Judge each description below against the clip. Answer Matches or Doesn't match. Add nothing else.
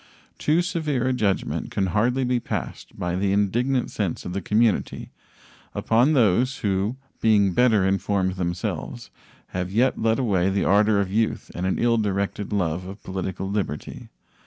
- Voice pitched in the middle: Doesn't match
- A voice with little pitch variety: Doesn't match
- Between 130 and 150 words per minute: Doesn't match